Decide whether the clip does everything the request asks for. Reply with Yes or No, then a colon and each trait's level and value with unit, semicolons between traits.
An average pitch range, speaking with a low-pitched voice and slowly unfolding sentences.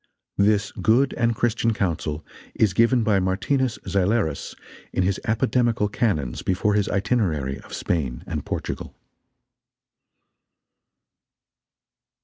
Yes: average, 4.2 semitones; low, 105 Hz; slow, 105 wpm